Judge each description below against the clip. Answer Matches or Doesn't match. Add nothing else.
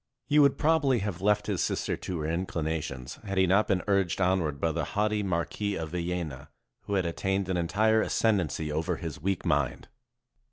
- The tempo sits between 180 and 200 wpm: Matches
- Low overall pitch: Matches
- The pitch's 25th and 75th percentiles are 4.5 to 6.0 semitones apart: Doesn't match